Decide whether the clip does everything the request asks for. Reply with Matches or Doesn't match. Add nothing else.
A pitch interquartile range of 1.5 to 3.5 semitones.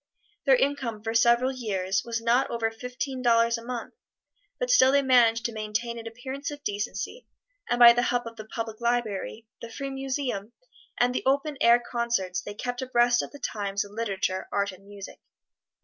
Matches